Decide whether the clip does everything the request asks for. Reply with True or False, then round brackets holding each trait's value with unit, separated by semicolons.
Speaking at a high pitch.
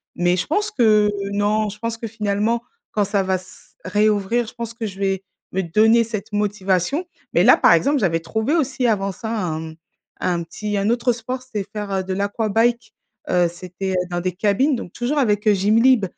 True (210 Hz)